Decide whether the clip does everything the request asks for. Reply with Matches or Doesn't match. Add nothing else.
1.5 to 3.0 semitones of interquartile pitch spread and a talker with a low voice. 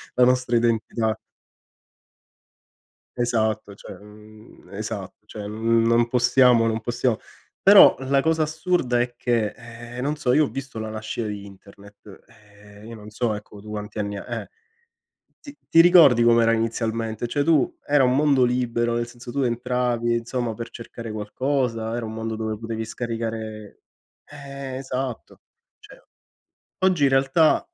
Matches